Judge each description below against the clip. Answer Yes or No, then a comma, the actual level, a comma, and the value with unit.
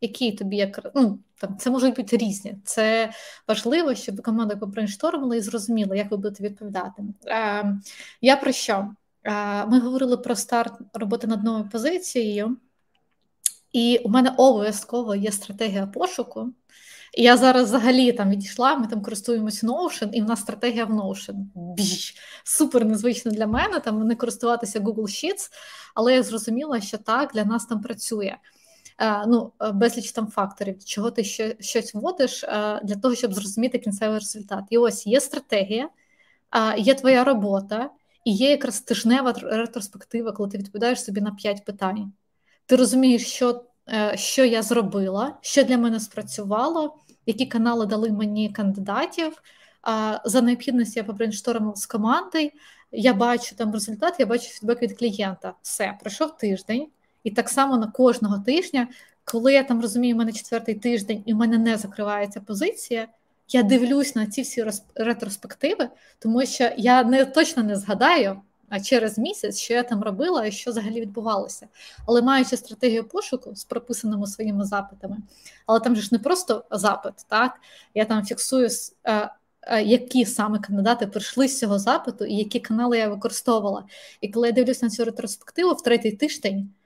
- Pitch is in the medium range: No, high, 230 Hz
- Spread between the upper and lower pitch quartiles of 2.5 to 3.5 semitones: Yes, average, 2.9 semitones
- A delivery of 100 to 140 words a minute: No, fast, 155 wpm